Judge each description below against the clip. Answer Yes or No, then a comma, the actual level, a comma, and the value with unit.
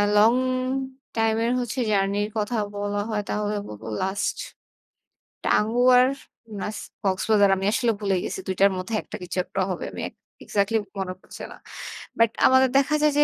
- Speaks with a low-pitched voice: No, high, 210 Hz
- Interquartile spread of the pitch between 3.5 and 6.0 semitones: No, average, 2.9 semitones